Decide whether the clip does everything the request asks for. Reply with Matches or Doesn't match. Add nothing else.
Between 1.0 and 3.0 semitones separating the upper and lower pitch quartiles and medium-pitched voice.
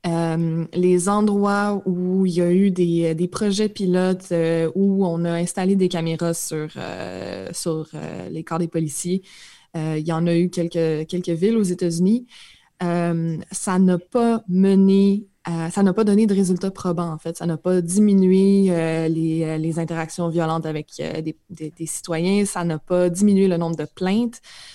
Matches